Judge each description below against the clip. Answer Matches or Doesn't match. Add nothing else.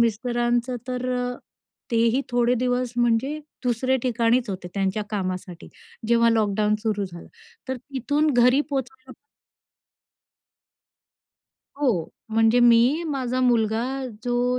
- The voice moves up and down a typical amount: Doesn't match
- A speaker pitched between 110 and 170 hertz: Doesn't match